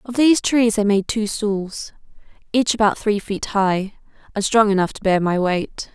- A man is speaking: No, female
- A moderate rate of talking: Yes, average, 190 wpm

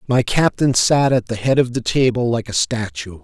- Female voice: No, male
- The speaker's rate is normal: No, fast, 220 wpm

